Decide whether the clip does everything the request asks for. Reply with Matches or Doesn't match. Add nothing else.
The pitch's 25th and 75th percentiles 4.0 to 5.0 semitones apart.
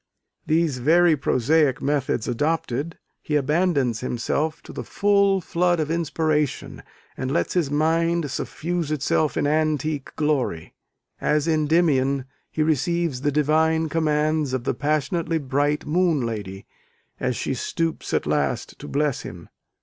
Doesn't match